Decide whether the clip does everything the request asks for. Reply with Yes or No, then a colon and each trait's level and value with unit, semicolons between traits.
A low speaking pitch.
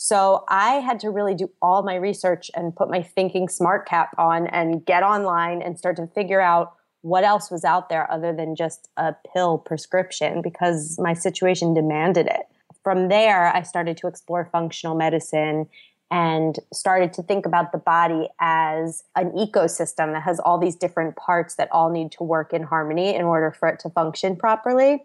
No: medium, 175 Hz